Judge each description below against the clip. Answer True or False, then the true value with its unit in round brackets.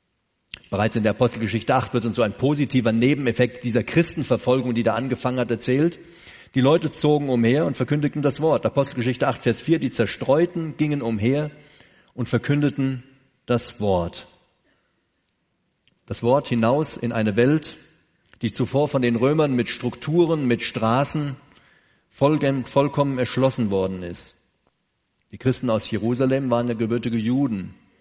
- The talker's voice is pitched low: True (125 Hz)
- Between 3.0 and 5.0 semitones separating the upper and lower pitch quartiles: True (3.4 semitones)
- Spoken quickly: False (140 wpm)